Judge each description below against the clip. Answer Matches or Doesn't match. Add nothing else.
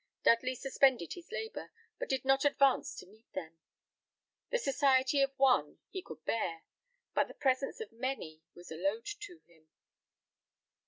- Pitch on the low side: Doesn't match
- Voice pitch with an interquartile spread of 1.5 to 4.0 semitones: Doesn't match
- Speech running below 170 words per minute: Matches